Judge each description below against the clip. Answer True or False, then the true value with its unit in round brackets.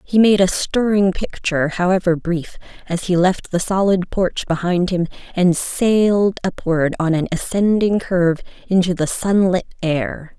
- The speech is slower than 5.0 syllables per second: True (4.4 syllables/s)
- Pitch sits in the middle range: True (180 Hz)